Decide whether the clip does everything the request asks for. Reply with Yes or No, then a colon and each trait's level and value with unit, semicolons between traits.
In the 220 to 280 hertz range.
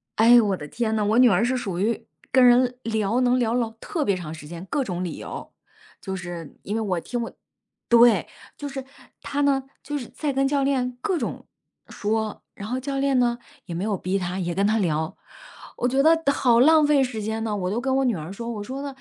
Yes: high, 230 Hz